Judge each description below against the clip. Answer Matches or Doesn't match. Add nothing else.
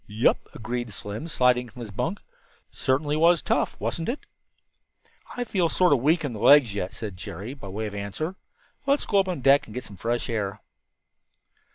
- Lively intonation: Matches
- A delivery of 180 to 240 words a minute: Matches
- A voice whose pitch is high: Doesn't match